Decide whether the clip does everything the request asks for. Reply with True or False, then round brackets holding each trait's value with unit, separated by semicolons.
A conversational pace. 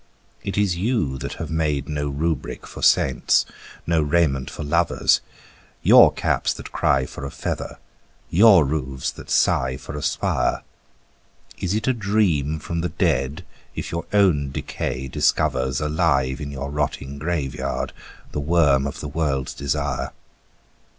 True (145 wpm)